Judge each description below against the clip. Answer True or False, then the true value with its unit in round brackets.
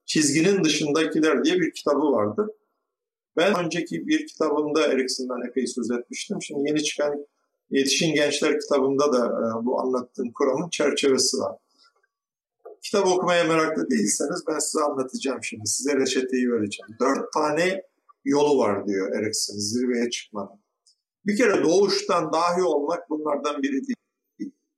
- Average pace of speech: True (130 wpm)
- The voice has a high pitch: False (150 Hz)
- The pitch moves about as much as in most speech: False (6.8 semitones)